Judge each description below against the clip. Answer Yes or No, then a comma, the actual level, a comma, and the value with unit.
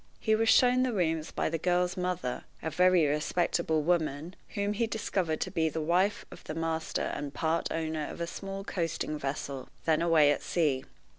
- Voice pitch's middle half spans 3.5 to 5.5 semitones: No, average, 2.9 semitones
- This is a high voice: No, medium, 165 Hz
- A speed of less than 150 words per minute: No, average, 190 wpm